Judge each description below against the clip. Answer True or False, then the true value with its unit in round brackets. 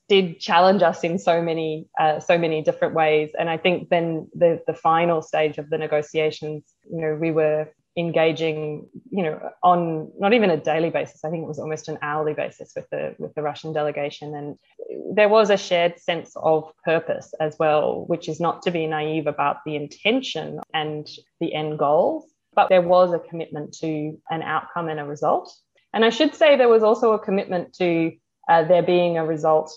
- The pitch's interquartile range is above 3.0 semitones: False (2.6 semitones)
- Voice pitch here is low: False (160 Hz)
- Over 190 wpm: True (200 wpm)